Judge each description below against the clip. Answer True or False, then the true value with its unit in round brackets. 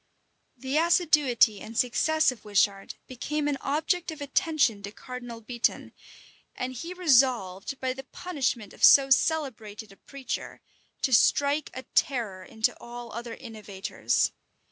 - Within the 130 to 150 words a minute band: True (140 wpm)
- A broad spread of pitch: False (4.5 semitones)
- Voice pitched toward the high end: True (255 Hz)